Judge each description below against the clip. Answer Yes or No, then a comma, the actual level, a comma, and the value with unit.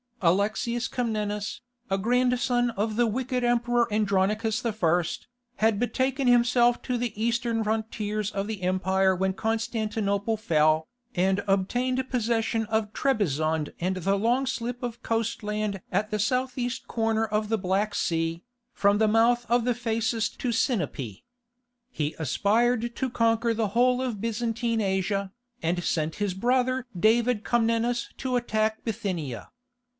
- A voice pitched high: Yes, high, 220 Hz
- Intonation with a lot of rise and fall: No, average, 3.3 semitones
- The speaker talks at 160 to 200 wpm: No, average, 140 wpm